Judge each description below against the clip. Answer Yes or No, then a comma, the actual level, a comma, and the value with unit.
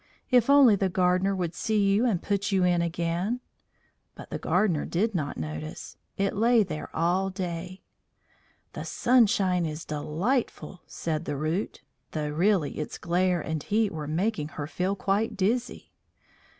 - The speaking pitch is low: No, medium, 185 Hz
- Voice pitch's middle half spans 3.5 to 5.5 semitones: Yes, average, 4.2 semitones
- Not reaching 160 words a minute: Yes, average, 150 wpm